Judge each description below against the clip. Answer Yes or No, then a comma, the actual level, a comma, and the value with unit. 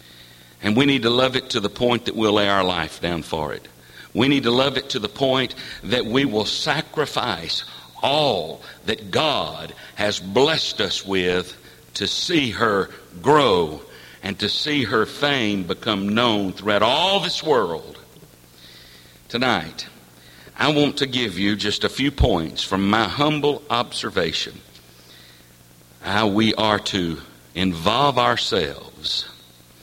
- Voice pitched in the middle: No, low, 105 Hz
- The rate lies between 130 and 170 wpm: Yes, average, 145 wpm